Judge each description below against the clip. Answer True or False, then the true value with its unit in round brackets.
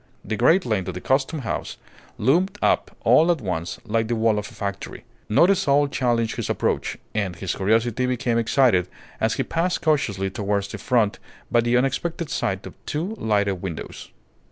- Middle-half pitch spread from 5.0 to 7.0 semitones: True (5.5 semitones)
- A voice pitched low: True (115 Hz)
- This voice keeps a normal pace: True (180 wpm)